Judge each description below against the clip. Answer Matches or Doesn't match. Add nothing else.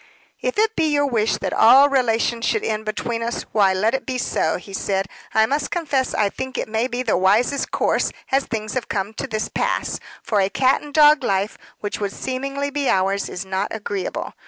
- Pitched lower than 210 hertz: Doesn't match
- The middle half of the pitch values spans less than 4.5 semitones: Doesn't match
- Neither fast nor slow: Doesn't match